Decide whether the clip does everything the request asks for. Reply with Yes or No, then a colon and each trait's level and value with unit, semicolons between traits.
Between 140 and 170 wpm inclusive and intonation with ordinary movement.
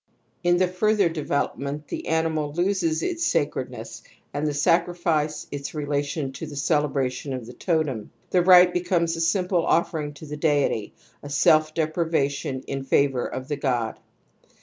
Yes: average, 150 wpm; average, 3.2 semitones